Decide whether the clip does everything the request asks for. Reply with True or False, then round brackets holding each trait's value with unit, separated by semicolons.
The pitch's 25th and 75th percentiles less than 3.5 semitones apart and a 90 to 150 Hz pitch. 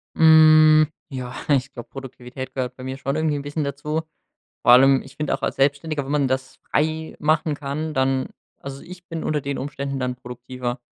True (2.8 semitones; 140 Hz)